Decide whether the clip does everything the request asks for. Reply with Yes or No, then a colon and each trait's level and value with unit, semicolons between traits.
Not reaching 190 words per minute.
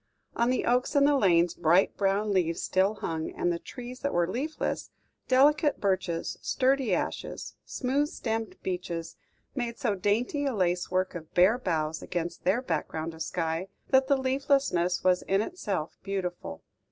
Yes: average, 155 wpm